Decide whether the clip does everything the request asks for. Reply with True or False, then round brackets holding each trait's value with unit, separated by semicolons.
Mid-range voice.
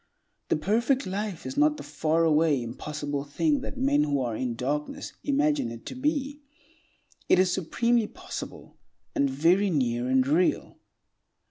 True (165 Hz)